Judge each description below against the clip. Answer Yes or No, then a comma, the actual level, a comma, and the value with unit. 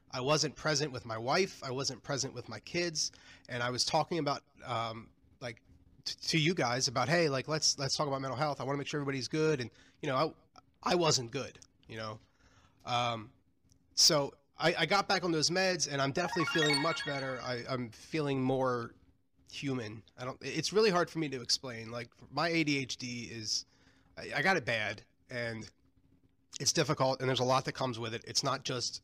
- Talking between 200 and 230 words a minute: Yes, fast, 205 wpm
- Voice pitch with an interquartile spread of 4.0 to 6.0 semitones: Yes, average, 4.5 semitones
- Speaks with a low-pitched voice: Yes, low, 130 Hz